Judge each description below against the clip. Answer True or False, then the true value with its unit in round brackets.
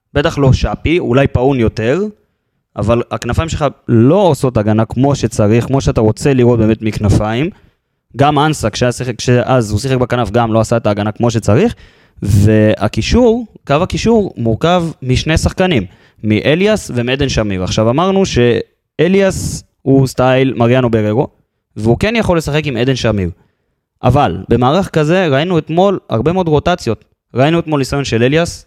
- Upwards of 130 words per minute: True (145 wpm)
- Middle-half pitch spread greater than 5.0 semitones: True (5.6 semitones)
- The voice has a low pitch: True (125 Hz)